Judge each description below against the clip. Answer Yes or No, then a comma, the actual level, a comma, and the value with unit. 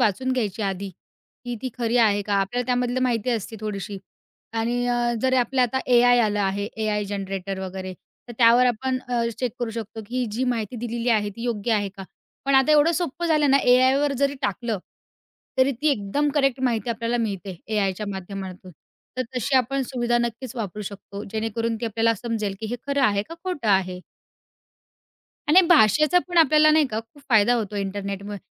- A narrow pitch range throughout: No, average, 3.9 semitones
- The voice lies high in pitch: Yes, high, 230 Hz